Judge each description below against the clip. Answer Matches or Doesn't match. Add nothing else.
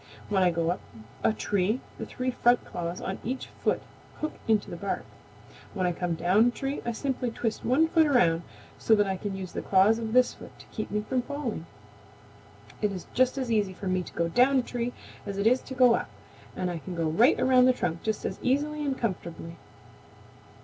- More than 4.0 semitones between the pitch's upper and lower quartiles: Matches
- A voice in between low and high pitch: Doesn't match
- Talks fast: Matches